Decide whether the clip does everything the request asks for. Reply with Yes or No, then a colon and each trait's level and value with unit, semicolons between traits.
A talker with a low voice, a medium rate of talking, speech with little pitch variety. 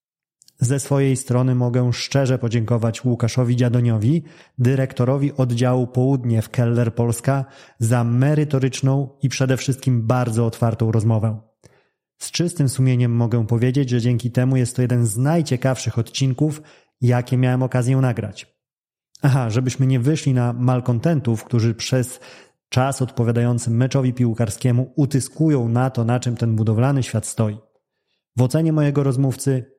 Yes: low, 125 Hz; average, 130 wpm; narrow, 2.2 semitones